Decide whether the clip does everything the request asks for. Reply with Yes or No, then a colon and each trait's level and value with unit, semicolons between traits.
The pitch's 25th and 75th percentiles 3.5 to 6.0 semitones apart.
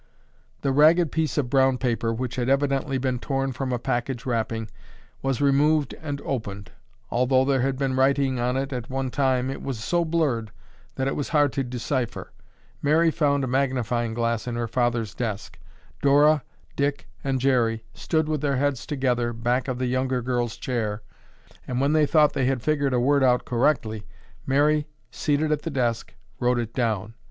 No: average, 2.8 semitones